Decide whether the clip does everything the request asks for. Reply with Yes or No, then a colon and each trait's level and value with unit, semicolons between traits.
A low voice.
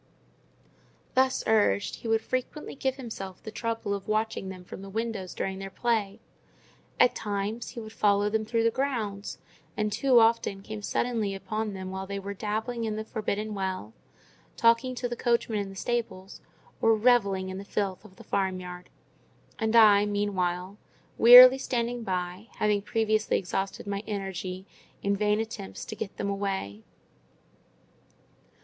No: high, 210 Hz